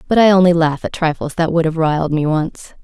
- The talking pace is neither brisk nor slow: No, fast, 255 wpm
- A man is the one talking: No, female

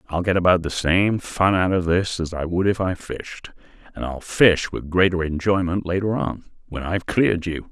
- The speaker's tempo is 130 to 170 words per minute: No, average, 195 wpm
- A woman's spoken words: No, male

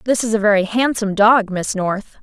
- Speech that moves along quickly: Yes, fast, 215 wpm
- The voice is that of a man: No, female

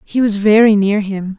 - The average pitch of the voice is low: No, high, 205 Hz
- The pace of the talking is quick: Yes, fast, 215 wpm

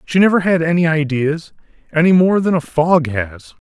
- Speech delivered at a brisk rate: No, average, 180 wpm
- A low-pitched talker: No, medium, 155 Hz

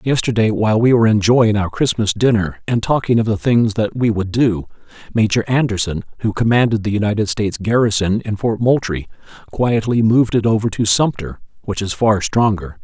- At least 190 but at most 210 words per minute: No, average, 180 wpm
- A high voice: No, low, 110 Hz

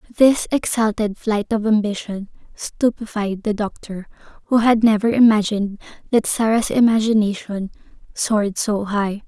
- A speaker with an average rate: No, slow, 115 wpm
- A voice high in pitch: Yes, high, 215 Hz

